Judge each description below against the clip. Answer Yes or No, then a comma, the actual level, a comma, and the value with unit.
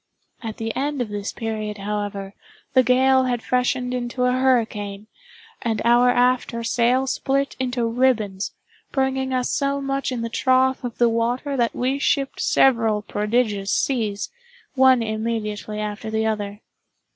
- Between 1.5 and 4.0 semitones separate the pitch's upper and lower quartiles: Yes, average, 3.1 semitones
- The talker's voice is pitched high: Yes, high, 240 Hz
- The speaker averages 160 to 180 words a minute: No, average, 145 wpm